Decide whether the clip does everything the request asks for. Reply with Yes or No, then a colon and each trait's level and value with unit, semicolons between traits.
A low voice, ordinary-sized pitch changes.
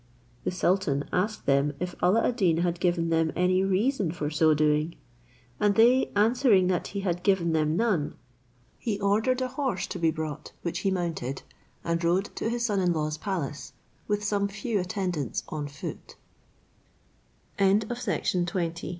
No: medium, 180 Hz; average, 4.2 semitones